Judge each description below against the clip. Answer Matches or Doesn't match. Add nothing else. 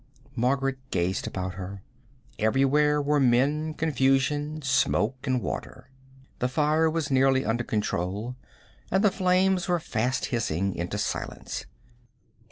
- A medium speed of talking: Doesn't match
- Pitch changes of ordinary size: Matches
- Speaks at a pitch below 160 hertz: Matches